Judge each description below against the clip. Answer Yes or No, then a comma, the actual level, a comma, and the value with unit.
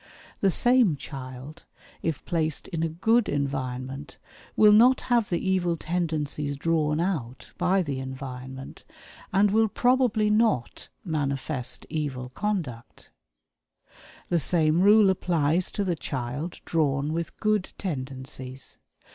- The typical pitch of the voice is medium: Yes, medium, 160 Hz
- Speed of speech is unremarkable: No, slow, 120 wpm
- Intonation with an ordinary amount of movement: No, wide, 5.9 semitones